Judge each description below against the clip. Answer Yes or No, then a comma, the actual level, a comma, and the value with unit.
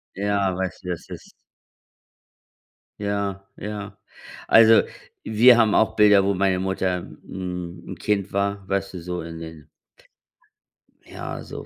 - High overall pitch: No, low, 100 Hz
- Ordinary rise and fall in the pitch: No, narrow, 2.1 semitones